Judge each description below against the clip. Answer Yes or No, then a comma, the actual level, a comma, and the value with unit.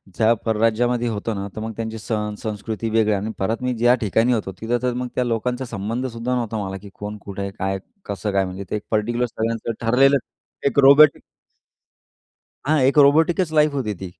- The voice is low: Yes, low, 115 Hz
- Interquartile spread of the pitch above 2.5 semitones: Yes, average, 2.9 semitones